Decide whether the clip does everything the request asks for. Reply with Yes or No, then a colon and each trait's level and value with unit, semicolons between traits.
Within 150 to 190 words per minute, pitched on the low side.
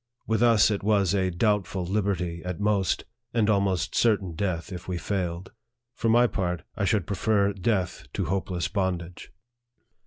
Yes: average, 155 wpm; very low, 95 Hz